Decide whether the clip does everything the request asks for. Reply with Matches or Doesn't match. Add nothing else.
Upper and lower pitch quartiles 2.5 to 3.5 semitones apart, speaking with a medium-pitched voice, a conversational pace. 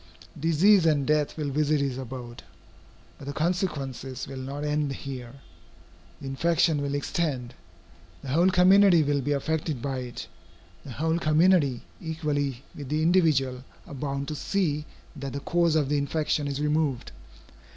Matches